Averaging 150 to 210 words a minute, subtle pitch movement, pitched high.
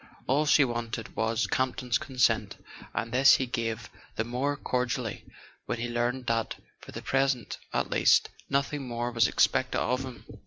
No: average, 165 wpm; narrow, 2.1 semitones; low, 125 Hz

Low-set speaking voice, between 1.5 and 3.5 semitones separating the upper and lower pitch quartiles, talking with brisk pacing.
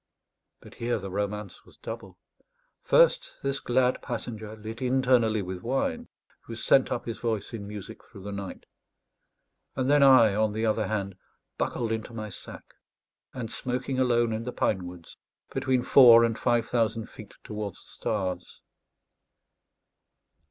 No: low, 115 Hz; average, 3.0 semitones; average, 150 wpm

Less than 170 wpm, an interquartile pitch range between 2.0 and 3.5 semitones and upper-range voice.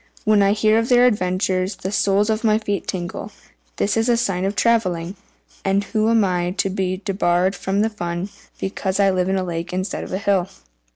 No: average, 195 wpm; narrow, 2.6 semitones; high, 195 Hz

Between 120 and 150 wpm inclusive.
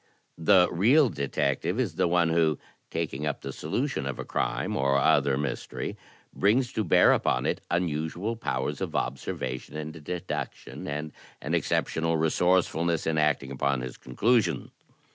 Yes: average, 145 wpm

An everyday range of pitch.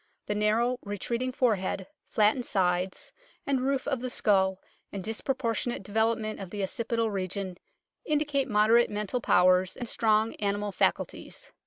Yes: average, 3.5 semitones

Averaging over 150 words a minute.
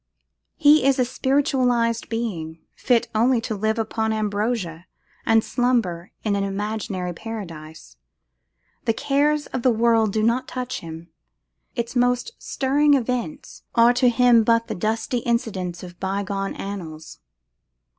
No: slow, 135 wpm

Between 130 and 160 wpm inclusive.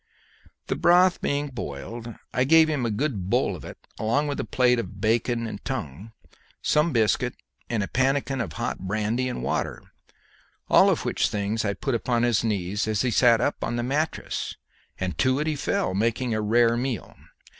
No: average, 185 wpm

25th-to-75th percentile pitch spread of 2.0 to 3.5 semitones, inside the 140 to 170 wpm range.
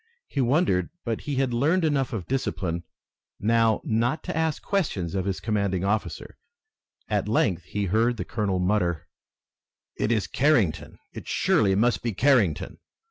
No: average, 5.3 semitones; average, 150 wpm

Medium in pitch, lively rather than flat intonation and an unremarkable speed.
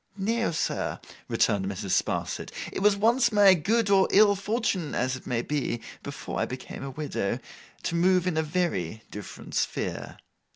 Yes: medium, 175 Hz; wide, 8.0 semitones; average, 155 wpm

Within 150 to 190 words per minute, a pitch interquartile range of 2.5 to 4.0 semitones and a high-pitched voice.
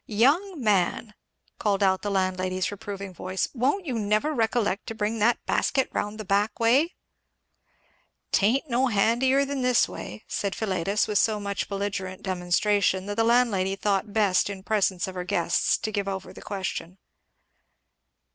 Yes: average, 155 wpm; average, 3.2 semitones; high, 205 Hz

